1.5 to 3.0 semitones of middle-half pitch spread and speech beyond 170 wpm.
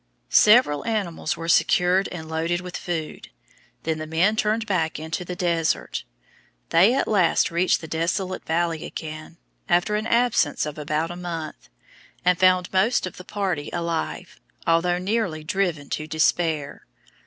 No: average, 2.7 semitones; average, 150 wpm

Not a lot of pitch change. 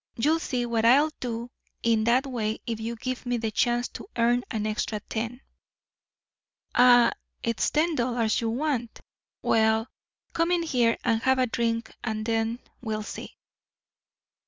Yes: narrow, 2.0 semitones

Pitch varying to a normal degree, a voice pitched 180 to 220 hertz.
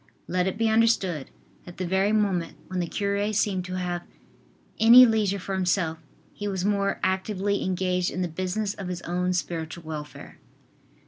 No: narrow, 2.3 semitones; medium, 185 Hz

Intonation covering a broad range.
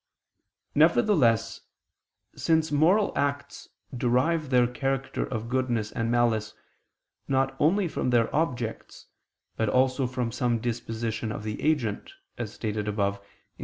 No: average, 3.7 semitones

